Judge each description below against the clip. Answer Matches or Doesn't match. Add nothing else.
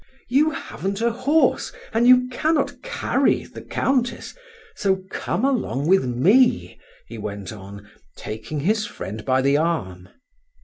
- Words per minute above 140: Doesn't match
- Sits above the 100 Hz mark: Matches